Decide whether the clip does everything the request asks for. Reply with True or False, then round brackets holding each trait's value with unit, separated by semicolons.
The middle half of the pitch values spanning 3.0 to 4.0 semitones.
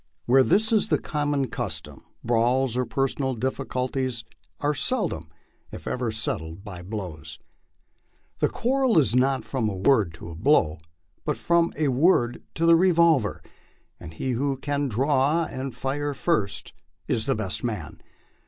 False (5.2 semitones)